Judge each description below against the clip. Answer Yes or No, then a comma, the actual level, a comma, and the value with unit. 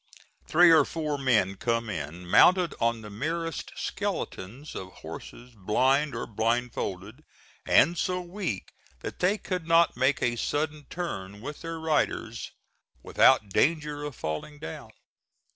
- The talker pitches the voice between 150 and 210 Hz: No, low, 135 Hz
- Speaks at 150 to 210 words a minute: No, average, 140 wpm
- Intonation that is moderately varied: No, wide, 7.1 semitones